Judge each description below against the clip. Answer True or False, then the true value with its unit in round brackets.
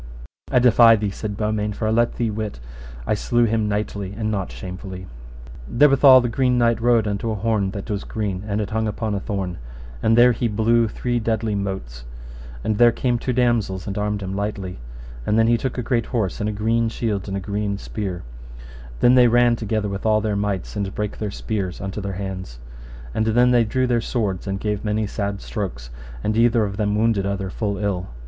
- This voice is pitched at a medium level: False (105 Hz)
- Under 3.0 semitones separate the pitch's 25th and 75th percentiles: True (2.6 semitones)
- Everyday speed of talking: False (210 wpm)